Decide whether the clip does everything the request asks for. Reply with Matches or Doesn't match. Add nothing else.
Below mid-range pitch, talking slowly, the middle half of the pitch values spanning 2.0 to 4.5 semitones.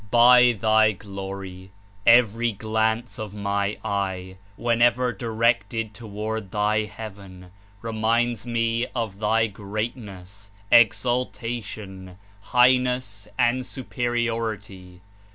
Matches